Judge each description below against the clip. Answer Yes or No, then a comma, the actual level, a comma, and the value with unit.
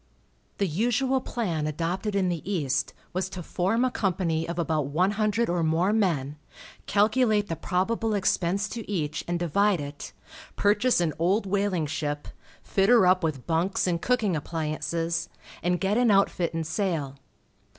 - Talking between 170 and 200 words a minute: No, average, 160 wpm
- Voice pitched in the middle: Yes, medium, 180 Hz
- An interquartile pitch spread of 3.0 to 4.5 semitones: Yes, average, 4.1 semitones